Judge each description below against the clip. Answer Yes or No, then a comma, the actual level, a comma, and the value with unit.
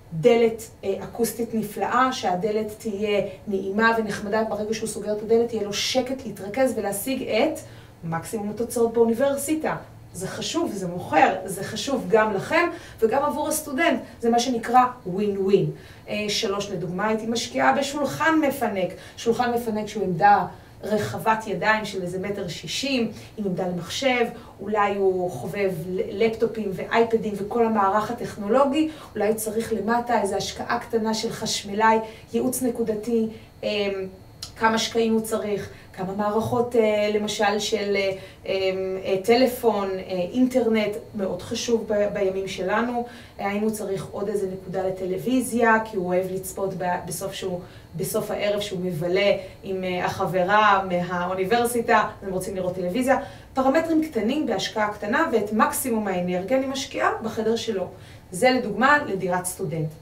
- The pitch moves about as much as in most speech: Yes, average, 3.2 semitones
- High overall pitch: Yes, high, 215 Hz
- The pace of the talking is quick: No, average, 125 wpm